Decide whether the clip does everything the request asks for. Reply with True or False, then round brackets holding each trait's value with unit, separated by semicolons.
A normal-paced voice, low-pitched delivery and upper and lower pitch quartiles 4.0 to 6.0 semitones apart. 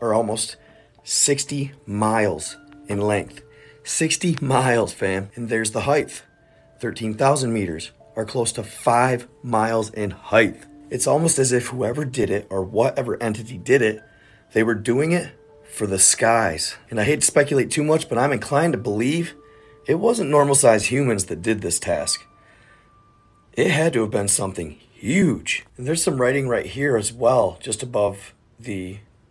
True (165 wpm; 120 Hz; 5.0 semitones)